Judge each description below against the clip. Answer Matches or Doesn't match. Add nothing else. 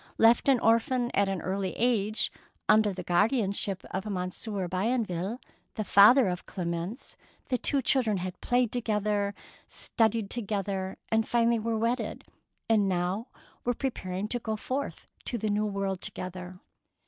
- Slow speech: Doesn't match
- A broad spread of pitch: Doesn't match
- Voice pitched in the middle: Doesn't match